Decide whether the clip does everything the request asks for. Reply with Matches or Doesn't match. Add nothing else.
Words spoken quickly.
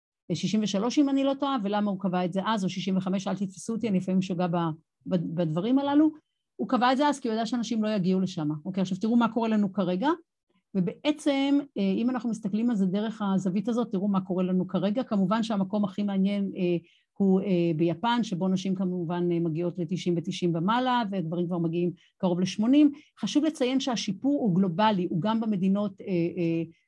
Matches